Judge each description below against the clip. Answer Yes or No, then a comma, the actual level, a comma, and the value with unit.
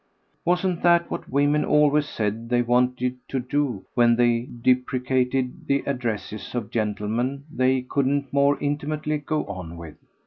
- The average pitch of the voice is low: Yes, low, 130 Hz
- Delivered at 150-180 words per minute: No, average, 140 wpm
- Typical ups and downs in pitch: Yes, average, 3.3 semitones